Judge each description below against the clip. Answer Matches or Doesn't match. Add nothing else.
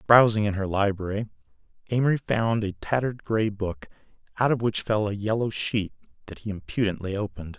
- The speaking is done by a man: Matches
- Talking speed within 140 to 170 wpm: Matches